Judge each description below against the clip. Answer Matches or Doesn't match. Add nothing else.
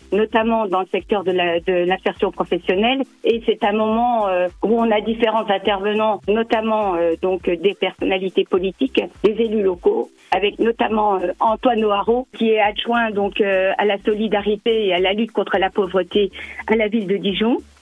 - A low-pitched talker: Doesn't match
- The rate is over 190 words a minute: Doesn't match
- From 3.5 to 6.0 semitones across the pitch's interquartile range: Doesn't match